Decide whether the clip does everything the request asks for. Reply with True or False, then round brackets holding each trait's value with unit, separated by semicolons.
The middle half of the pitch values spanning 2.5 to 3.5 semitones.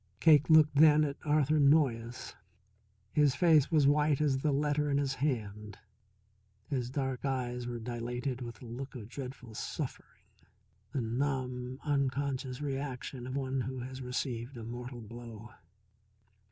True (2.8 semitones)